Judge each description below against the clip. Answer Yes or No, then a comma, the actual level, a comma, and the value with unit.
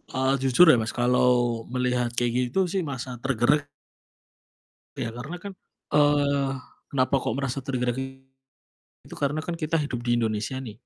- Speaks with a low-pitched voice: Yes, low, 130 Hz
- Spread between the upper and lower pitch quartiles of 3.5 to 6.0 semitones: No, average, 2.7 semitones